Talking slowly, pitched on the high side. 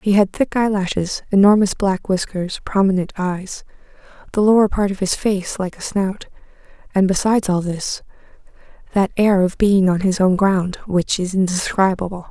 No: average, 160 wpm; high, 195 Hz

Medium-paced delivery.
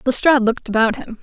Yes: average, 195 wpm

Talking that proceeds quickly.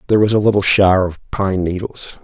Yes: fast, 215 wpm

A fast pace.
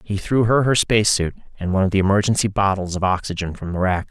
Yes: fast, 235 wpm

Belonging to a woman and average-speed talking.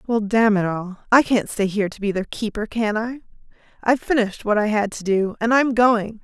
No: female; fast, 240 wpm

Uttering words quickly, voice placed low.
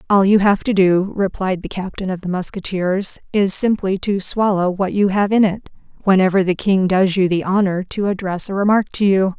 No: fast, 210 wpm; high, 190 Hz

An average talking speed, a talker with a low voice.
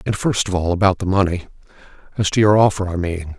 No: fast, 215 wpm; very low, 95 Hz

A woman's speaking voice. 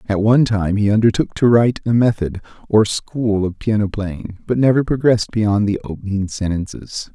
No: male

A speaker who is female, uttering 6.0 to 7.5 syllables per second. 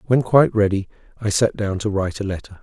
No: male; 6.4 syllables/s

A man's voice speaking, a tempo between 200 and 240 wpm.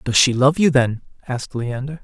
Yes: male; fast, 205 wpm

